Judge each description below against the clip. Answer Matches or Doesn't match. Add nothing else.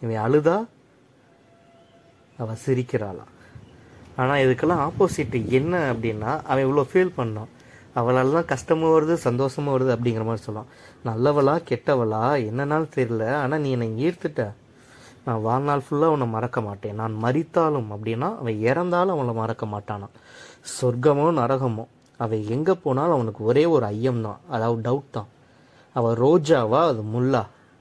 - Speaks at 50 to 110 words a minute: Doesn't match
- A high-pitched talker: Doesn't match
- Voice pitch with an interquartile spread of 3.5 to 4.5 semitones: Matches